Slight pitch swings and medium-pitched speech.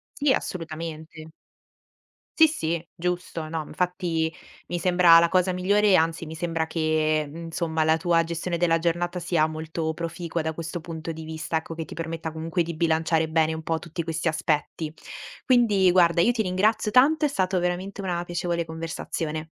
Yes: narrow, 1.8 semitones; medium, 165 Hz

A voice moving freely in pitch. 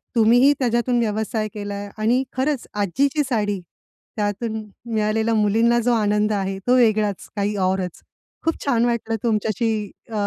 No: narrow, 2.4 semitones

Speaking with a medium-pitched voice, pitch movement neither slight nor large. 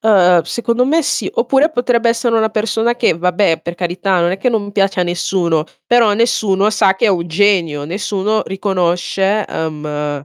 No: high, 195 Hz; average, 4.3 semitones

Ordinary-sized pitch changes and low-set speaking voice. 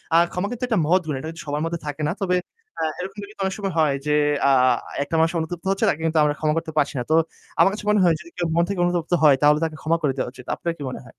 No: average, 3.2 semitones; medium, 165 Hz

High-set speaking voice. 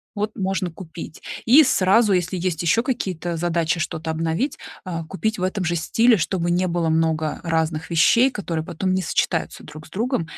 No: medium, 175 Hz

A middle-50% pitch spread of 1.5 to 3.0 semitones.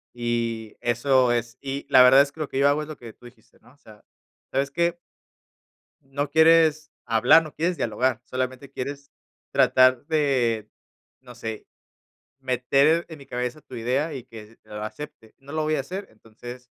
No: average, 3.6 semitones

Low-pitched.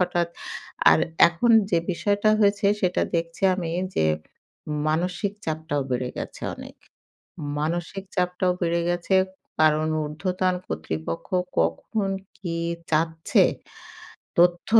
No: medium, 170 Hz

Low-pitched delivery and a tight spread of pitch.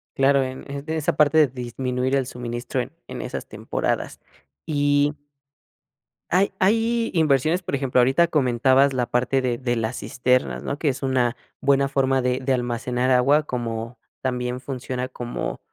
Yes: low, 130 Hz; narrow, 2.3 semitones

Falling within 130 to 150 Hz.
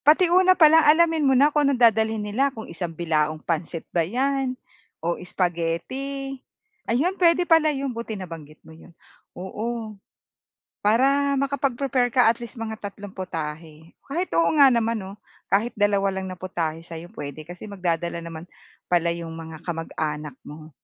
No: high, 205 Hz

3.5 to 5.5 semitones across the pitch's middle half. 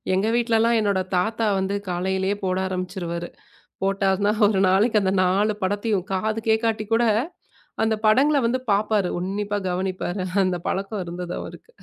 No: average, 2.8 semitones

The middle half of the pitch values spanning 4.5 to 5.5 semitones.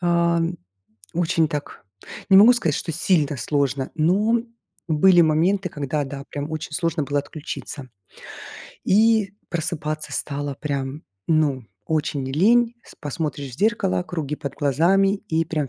No: average, 3.7 semitones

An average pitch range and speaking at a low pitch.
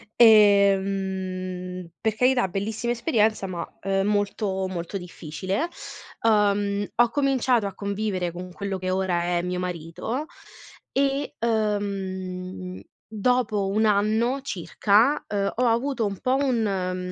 No: average, 3.4 semitones; high, 200 Hz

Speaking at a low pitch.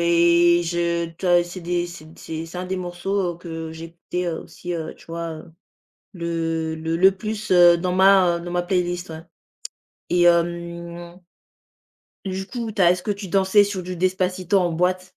No: medium, 175 Hz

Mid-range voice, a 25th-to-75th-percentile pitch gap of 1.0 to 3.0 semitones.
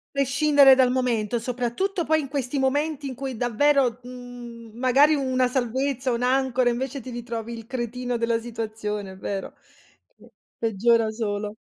No: high, 245 Hz; narrow, 2.5 semitones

